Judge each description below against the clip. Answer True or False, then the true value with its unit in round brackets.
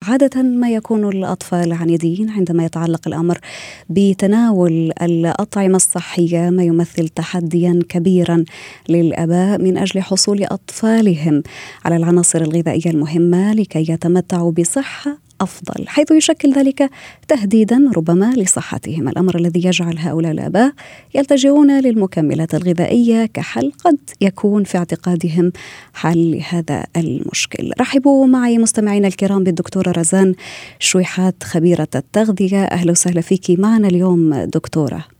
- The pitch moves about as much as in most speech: True (4.0 semitones)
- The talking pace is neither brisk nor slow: True (110 wpm)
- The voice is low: False (180 Hz)